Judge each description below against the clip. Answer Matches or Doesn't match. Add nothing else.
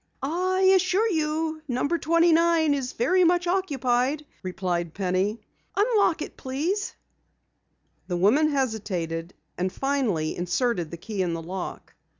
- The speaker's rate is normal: Doesn't match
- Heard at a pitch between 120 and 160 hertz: Doesn't match